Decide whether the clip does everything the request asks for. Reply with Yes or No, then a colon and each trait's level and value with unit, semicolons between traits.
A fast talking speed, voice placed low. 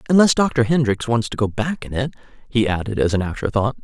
Yes: fast, 235 wpm; low, 120 Hz